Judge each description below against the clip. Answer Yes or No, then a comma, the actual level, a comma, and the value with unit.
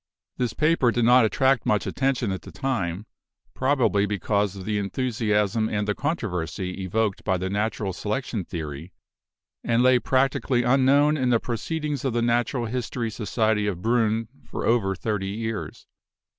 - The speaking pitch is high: No, low, 110 Hz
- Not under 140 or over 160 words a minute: Yes, average, 155 wpm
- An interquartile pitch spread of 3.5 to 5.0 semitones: Yes, average, 3.9 semitones